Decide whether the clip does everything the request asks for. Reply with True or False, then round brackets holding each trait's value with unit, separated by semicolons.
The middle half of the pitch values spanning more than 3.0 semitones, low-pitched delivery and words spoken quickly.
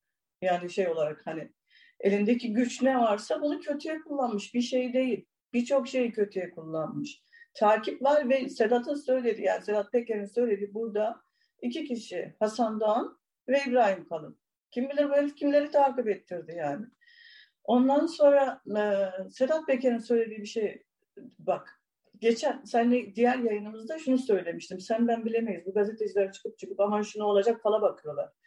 False (4.6 semitones; 235 Hz; 145 wpm)